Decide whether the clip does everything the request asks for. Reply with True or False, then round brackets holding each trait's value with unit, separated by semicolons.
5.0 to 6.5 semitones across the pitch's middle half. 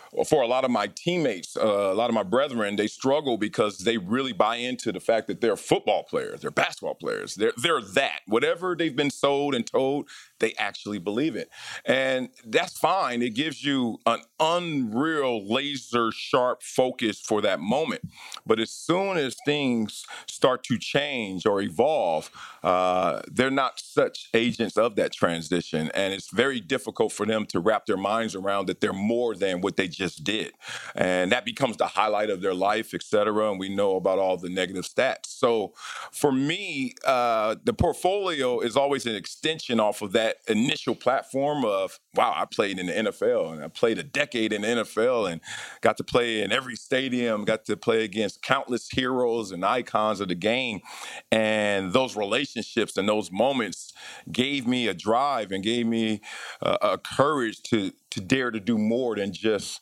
True (5.4 semitones)